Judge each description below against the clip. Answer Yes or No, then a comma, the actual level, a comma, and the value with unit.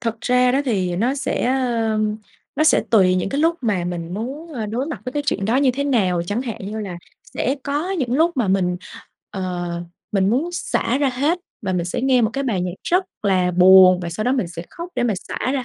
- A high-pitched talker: Yes, high, 230 Hz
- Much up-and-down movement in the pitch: Yes, wide, 6.4 semitones